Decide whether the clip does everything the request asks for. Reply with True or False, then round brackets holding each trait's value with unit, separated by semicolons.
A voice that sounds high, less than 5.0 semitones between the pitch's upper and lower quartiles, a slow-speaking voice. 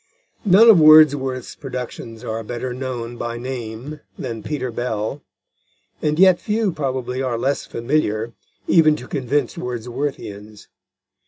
False (130 Hz; 4.3 semitones; 120 wpm)